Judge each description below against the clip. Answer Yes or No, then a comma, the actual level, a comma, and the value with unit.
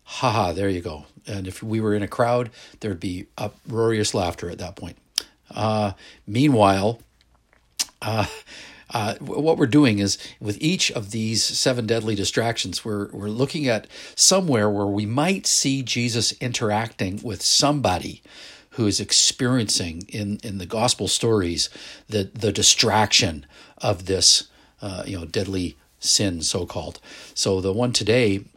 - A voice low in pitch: Yes, low, 105 Hz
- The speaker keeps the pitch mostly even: No, average, 3.7 semitones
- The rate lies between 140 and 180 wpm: Yes, average, 145 wpm